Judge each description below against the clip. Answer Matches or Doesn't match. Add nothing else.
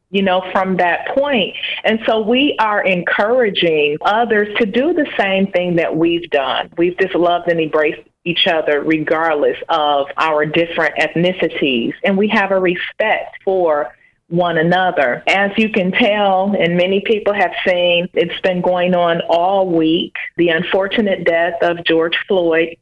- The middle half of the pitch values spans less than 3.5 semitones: Matches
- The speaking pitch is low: Doesn't match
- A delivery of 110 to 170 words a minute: Matches